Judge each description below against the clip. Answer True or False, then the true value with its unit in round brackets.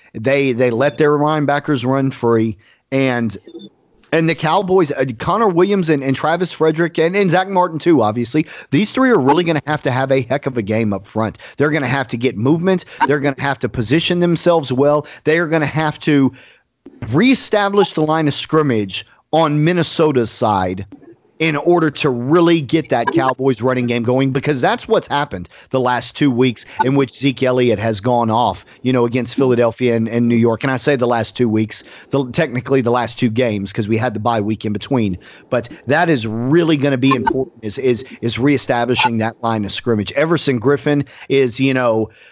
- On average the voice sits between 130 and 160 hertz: True (135 Hz)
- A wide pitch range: False (4.5 semitones)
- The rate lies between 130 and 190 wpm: False (205 wpm)